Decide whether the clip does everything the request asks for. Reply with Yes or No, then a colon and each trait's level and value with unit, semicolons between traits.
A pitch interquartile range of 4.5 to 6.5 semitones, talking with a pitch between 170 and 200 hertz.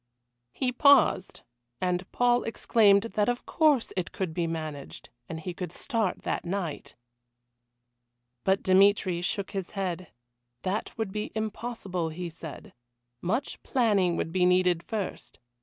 No: average, 3.7 semitones; high, 190 Hz